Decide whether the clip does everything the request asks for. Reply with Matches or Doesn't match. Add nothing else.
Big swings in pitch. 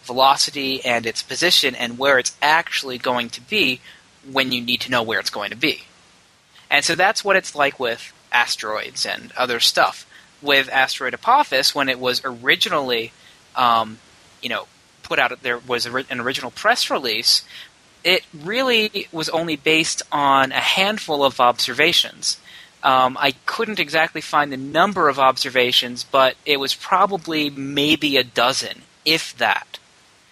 Doesn't match